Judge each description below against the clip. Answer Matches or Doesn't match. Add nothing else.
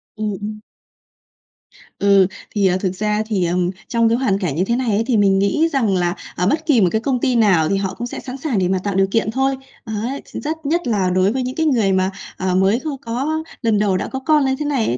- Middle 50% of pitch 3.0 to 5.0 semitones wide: Doesn't match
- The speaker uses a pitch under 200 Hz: Doesn't match